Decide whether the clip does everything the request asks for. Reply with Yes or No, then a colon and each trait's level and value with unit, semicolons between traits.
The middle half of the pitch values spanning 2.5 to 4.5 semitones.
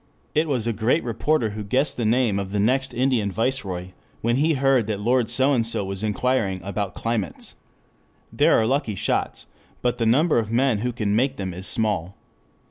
Yes: average, 4.1 semitones